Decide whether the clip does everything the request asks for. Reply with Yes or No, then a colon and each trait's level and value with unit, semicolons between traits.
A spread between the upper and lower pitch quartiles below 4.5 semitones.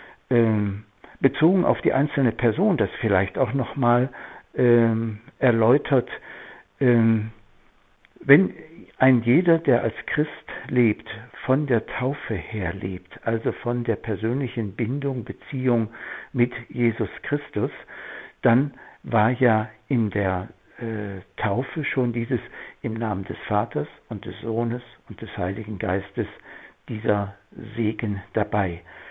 Yes: average, 2.9 semitones